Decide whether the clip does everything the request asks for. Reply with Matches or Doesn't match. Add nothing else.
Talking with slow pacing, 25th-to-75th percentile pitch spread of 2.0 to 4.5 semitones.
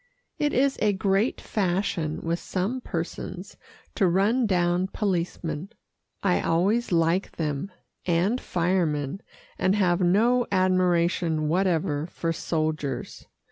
Matches